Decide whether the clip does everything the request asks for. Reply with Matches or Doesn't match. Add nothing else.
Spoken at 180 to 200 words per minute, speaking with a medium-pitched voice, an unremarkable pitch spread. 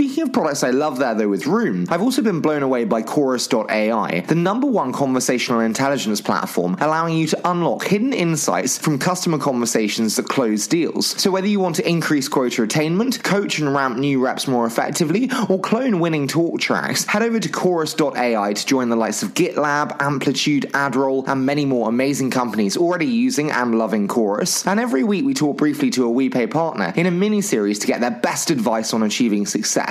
Doesn't match